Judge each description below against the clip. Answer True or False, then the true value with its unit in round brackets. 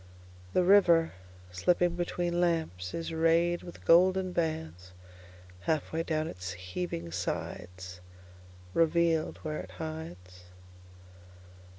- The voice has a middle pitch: True (155 Hz)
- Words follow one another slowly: True (85 wpm)